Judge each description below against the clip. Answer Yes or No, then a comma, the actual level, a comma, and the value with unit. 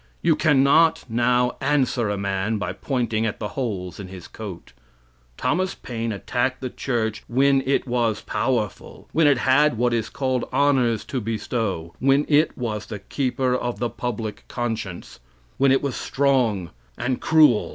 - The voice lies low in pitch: Yes, low, 120 Hz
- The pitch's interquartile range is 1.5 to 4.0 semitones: Yes, average, 3.7 semitones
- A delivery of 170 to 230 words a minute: No, average, 160 wpm